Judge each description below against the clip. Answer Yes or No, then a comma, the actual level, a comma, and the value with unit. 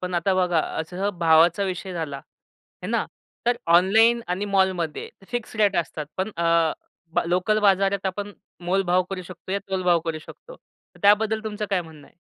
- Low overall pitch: No, medium, 185 Hz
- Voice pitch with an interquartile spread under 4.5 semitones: Yes, average, 2.8 semitones